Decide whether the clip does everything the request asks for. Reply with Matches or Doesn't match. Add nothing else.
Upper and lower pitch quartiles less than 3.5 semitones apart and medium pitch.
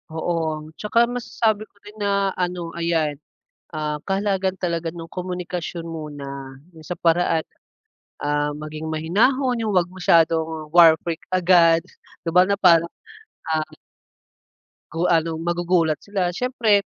Matches